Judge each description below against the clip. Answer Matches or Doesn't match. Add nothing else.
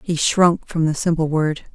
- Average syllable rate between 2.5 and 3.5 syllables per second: Doesn't match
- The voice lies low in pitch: Doesn't match